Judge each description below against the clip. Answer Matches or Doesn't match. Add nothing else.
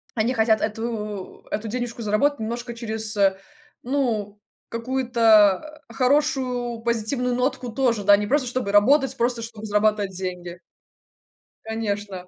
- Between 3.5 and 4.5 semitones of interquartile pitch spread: Doesn't match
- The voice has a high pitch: Matches